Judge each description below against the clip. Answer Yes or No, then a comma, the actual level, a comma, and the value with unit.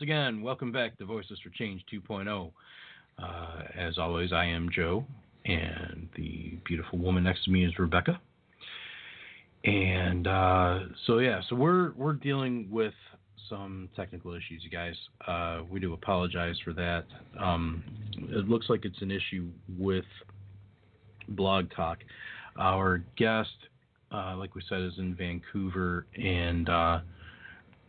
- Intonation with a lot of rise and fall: No, average, 3.3 semitones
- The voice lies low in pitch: Yes, very low, 95 Hz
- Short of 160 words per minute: Yes, average, 140 wpm